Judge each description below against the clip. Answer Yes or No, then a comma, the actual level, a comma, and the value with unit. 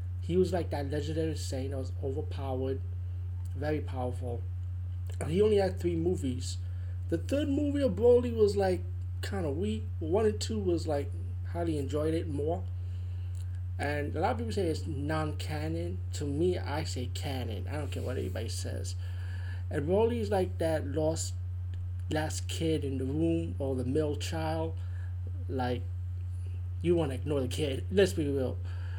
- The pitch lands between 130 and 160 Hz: No, very low, 90 Hz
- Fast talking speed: No, average, 170 wpm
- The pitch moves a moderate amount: No, narrow, 0.8 semitones